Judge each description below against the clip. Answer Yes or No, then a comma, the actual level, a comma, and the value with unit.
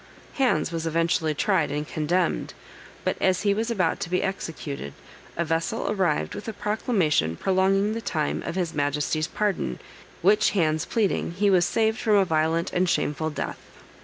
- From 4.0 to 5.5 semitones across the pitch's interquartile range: Yes, average, 4.4 semitones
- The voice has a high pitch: No, medium, 175 Hz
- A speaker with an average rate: Yes, average, 165 wpm